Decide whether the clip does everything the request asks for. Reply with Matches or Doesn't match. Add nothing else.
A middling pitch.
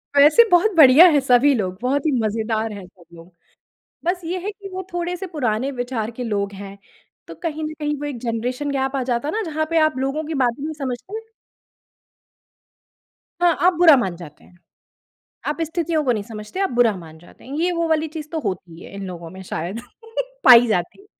Doesn't match